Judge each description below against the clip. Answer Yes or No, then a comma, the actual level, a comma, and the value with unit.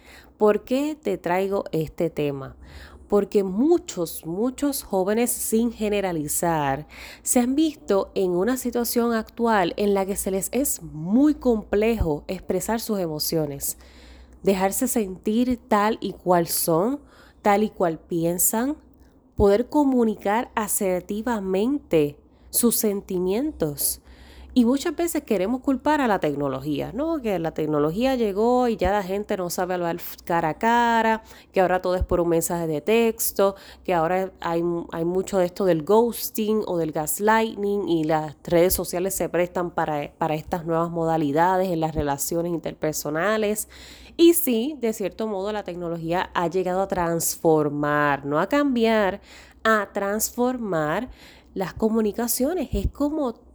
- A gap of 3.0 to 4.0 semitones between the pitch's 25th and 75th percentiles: No, average, 5.2 semitones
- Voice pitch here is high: Yes, high, 195 Hz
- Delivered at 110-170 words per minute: Yes, average, 140 wpm